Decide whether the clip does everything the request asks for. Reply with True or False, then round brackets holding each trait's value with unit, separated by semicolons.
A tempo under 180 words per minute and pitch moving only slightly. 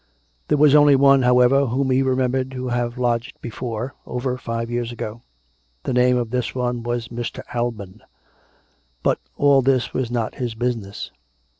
True (160 wpm; 1.7 semitones)